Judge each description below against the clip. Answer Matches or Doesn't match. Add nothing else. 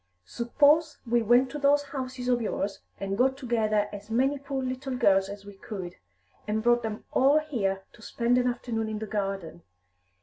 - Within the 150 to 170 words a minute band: Doesn't match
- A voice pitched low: Doesn't match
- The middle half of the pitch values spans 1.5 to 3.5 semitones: Doesn't match